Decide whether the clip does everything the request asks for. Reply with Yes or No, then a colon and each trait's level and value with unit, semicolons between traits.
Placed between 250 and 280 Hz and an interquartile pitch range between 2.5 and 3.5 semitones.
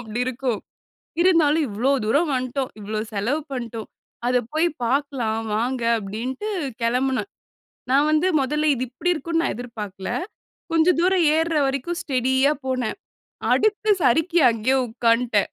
No: very high, 260 Hz; average, 4.9 semitones